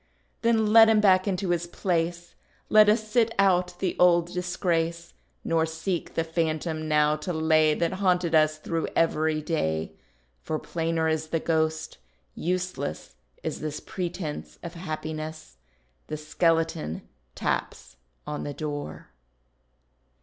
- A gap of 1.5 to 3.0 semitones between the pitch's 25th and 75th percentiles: Yes, narrow, 2.4 semitones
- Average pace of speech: No, slow, 130 wpm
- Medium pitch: Yes, medium, 165 Hz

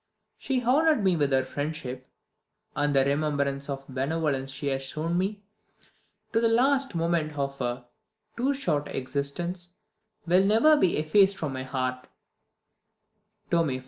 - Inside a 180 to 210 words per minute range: No, average, 145 wpm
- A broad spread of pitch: Yes, wide, 6.0 semitones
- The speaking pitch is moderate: Yes, medium, 155 Hz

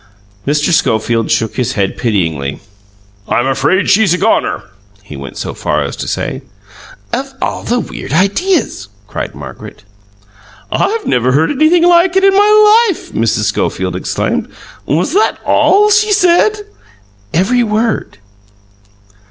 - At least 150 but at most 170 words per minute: No, slow, 135 wpm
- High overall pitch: Yes, high, 195 Hz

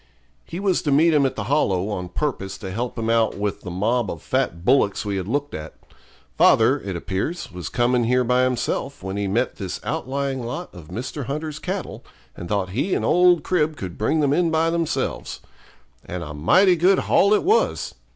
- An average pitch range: No, wide, 7.7 semitones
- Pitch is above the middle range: No, low, 125 Hz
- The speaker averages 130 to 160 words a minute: No, average, 200 wpm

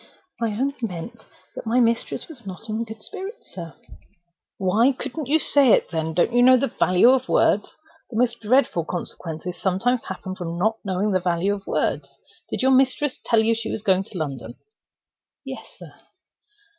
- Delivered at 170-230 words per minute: Yes, average, 180 wpm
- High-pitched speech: Yes, high, 220 Hz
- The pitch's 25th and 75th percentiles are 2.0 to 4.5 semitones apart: No, wide, 5.5 semitones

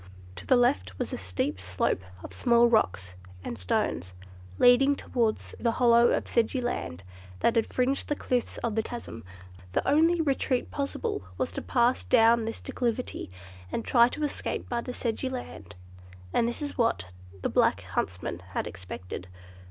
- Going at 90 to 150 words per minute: No, average, 165 wpm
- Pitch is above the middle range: Yes, high, 235 Hz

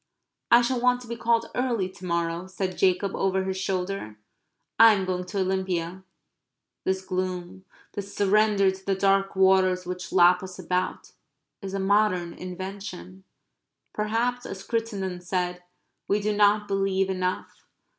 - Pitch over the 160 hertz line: Yes, high, 190 Hz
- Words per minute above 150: No, average, 145 wpm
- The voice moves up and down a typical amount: No, narrow, 1.8 semitones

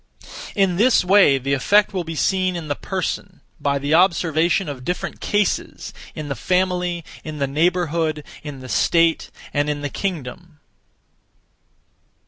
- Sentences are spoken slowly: No, average, 145 wpm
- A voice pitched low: No, medium, 165 Hz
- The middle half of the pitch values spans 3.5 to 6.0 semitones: Yes, average, 4.0 semitones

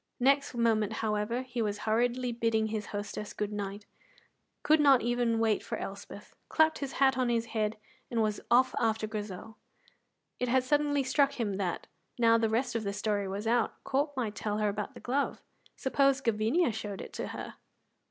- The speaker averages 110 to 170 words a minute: No, average, 180 wpm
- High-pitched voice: Yes, high, 230 Hz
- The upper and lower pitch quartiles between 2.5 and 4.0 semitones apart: Yes, average, 3.4 semitones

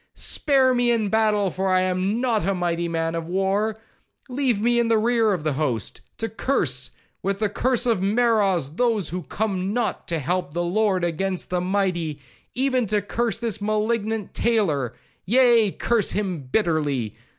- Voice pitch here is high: Yes, high, 200 Hz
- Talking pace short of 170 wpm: No, average, 175 wpm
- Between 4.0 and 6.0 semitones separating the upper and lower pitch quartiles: Yes, average, 4.7 semitones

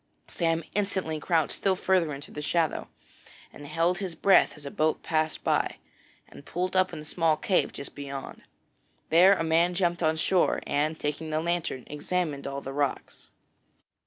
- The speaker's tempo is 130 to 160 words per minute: No, average, 170 wpm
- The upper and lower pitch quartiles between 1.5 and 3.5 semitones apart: Yes, average, 3.1 semitones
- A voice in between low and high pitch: Yes, medium, 160 Hz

